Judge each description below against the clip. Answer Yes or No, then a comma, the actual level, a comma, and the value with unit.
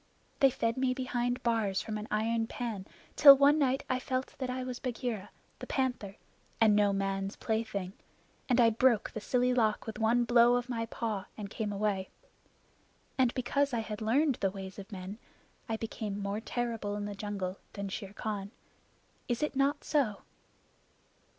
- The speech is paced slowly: No, average, 175 wpm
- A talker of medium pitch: No, high, 225 Hz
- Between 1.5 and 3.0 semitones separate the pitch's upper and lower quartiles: No, average, 3.6 semitones